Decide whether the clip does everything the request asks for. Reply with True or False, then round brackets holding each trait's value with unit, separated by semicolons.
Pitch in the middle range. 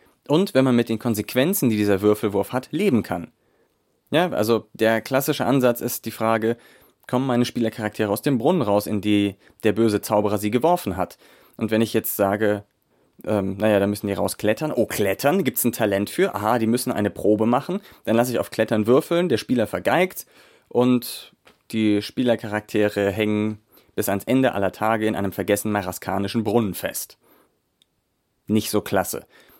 False (110 Hz)